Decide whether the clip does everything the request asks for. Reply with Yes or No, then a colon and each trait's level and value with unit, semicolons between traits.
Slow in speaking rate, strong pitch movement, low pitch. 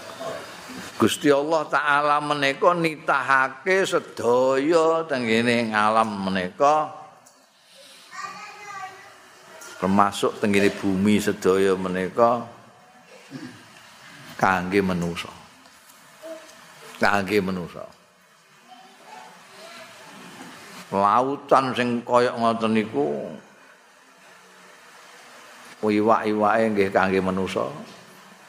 Yes: slow, 55 wpm; wide, 7.0 semitones; low, 120 Hz